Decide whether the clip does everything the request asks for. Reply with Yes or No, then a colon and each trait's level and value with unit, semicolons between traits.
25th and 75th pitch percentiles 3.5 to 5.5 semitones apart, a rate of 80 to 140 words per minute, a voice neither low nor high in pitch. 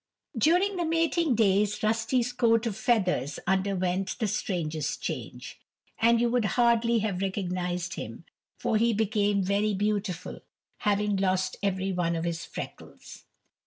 No: average, 3.8 semitones; slow, 135 wpm; high, 205 Hz